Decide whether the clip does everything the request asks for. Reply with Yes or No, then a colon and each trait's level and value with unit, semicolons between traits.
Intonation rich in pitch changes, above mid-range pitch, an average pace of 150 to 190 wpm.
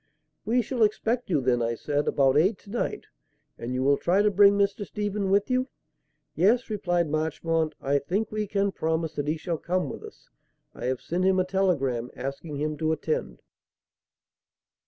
No: wide, 5.7 semitones; medium, 175 Hz; average, 180 wpm